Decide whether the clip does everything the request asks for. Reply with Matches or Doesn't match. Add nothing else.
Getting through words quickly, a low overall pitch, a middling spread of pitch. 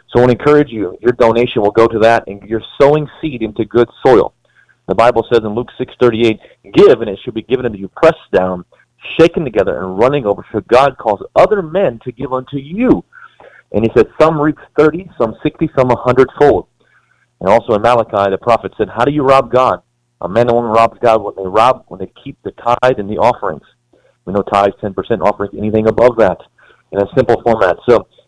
Matches